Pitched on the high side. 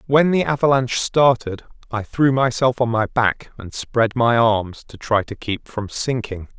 No: low, 120 Hz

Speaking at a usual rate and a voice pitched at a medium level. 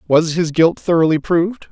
Yes: average, 175 wpm; medium, 165 Hz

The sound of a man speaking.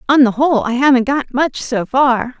No: female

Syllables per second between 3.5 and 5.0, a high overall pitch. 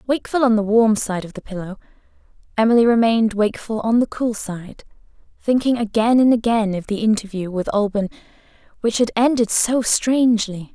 No: 5.5 syllables/s; high, 220 Hz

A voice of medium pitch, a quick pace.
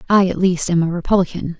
Yes: medium, 180 Hz; fast, 225 wpm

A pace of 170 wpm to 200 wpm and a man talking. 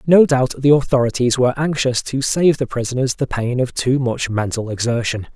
Yes: average, 190 wpm; male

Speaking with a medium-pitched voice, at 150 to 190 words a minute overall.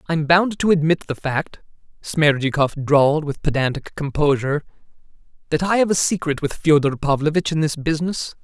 Yes: medium, 150 Hz; average, 155 wpm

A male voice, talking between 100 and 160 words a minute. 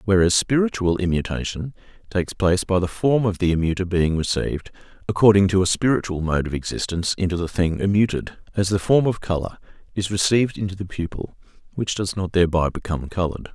No: male; average, 175 wpm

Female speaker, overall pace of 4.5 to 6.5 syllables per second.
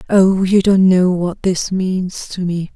No: female; 3.5 syllables/s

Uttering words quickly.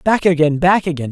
Yes: fast, 215 wpm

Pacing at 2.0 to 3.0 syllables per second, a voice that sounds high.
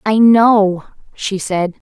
Yes: 2.9 syllables/s; high, 205 Hz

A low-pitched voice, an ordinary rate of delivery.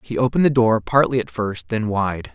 No: low, 110 Hz; fast, 230 wpm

